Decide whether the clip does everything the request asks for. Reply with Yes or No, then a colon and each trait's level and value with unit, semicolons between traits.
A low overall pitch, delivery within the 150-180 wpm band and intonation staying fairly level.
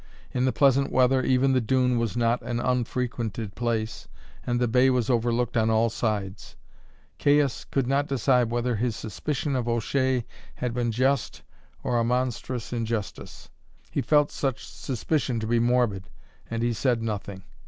Yes: low, 120 Hz; average, 160 wpm; narrow, 2.1 semitones